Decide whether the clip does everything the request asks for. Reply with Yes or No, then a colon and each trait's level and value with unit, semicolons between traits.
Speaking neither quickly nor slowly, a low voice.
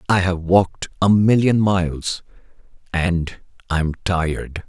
No: slow, 115 wpm; very low, 90 Hz